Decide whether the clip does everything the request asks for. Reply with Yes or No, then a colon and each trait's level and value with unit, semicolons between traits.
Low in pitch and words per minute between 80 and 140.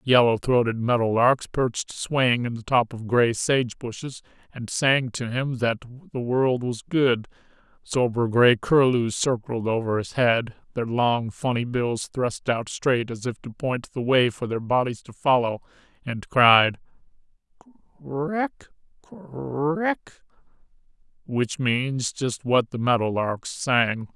No: low, 125 Hz; average, 155 wpm